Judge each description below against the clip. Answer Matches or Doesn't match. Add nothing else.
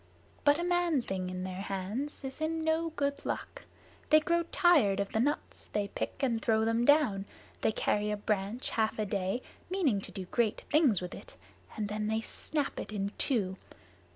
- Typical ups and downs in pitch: Doesn't match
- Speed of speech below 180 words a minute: Doesn't match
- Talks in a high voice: Matches